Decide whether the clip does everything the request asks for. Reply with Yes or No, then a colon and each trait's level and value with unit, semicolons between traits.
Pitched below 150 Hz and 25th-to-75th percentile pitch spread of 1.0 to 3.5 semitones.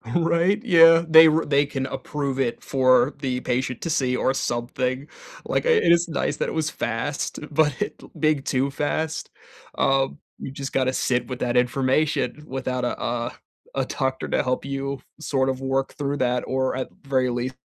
Yes: low, 135 Hz; average, 2.9 semitones